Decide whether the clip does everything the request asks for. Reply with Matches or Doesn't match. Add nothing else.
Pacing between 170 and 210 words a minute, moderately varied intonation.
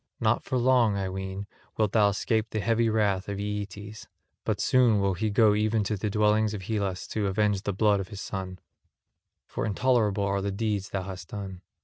Doesn't match